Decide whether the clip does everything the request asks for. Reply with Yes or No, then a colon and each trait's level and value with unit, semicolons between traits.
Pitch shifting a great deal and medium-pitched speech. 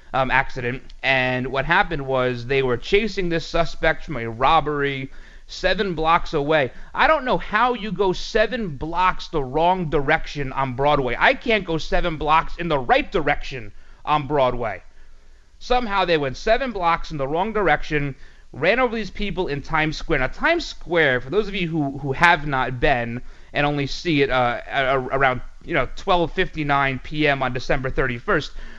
No: average, 5.0 semitones; medium, 155 Hz